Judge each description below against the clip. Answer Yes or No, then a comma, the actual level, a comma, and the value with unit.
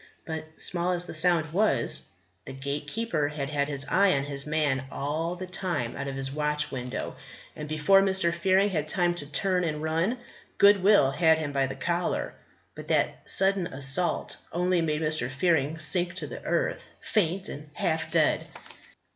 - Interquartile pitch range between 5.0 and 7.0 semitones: No, average, 3.7 semitones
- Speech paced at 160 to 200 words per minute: Yes, average, 170 wpm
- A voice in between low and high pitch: Yes, medium, 160 Hz